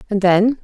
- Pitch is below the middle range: No, high, 210 Hz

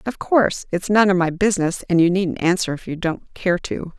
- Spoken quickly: Yes, fast, 240 wpm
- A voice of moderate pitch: Yes, medium, 180 Hz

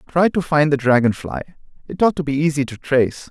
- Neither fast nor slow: No, fast, 220 wpm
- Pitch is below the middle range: No, medium, 145 Hz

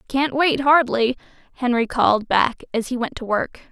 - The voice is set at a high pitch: Yes, very high, 250 Hz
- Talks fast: No, average, 180 wpm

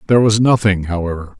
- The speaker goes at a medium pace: Yes, average, 170 wpm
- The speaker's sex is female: No, male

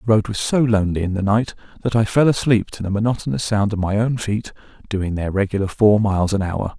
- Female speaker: No, male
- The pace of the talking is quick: Yes, fast, 240 wpm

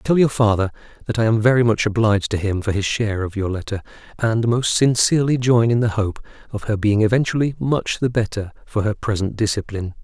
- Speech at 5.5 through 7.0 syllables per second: Yes, 5.9 syllables/s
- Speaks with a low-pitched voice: Yes, low, 110 Hz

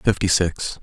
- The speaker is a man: Yes, male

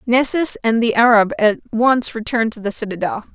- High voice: Yes, high, 230 Hz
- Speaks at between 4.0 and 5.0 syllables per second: No, 5.2 syllables/s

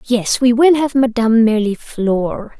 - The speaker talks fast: No, average, 140 wpm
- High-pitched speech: Yes, high, 235 Hz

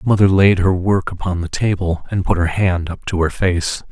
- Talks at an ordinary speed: No, fast, 245 wpm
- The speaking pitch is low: Yes, very low, 90 Hz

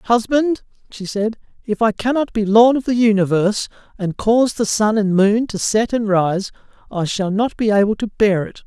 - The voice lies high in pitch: Yes, high, 215 Hz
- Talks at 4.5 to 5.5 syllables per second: Yes, 4.9 syllables/s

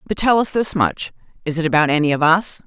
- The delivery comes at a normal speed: No, fast, 225 wpm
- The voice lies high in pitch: No, medium, 175 Hz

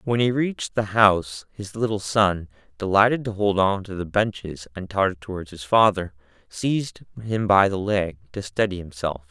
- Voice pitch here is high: No, low, 100 Hz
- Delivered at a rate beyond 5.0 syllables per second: No, 4.9 syllables/s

